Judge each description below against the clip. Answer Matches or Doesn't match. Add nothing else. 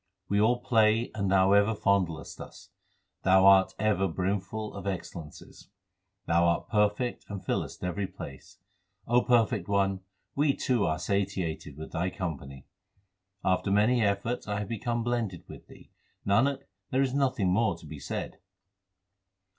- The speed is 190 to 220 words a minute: Doesn't match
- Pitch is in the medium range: Doesn't match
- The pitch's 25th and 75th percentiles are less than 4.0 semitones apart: Matches